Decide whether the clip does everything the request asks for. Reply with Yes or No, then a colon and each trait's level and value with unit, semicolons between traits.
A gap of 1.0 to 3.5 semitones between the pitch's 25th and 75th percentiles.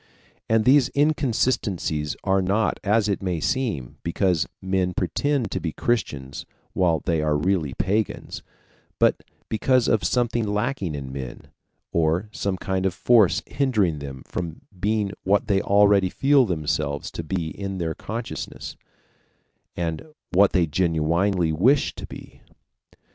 No: average, 5.1 semitones